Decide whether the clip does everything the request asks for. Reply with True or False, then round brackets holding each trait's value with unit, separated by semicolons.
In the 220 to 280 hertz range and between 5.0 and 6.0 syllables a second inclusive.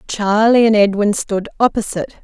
False (210 Hz; 5.2 syllables/s)